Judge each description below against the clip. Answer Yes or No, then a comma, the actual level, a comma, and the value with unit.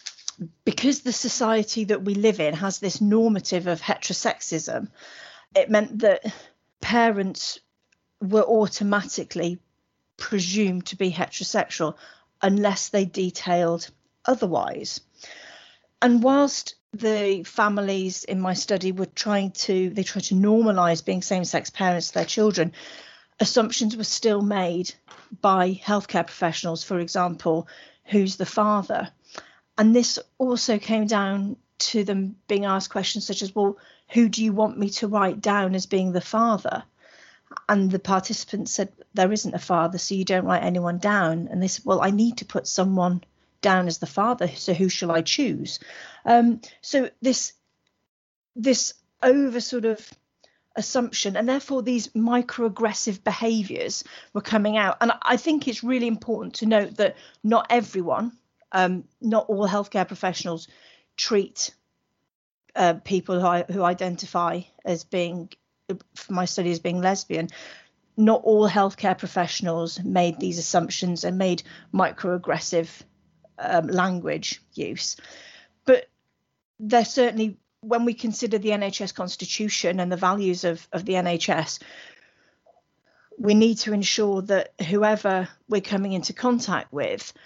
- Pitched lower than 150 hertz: No, high, 200 Hz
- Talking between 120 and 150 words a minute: Yes, average, 140 wpm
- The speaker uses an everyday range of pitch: Yes, average, 3.3 semitones